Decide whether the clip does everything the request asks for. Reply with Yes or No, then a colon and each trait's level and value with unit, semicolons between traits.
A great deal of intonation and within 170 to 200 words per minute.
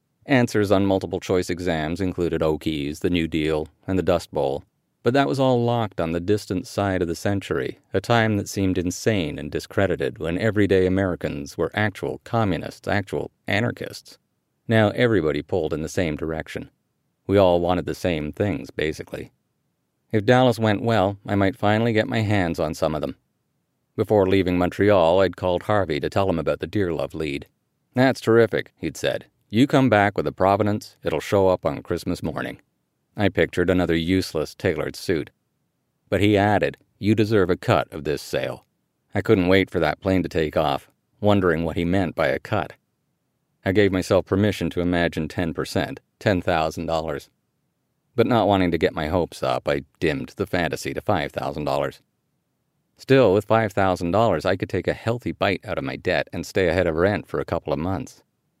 No: average, 3.8 semitones; average, 180 wpm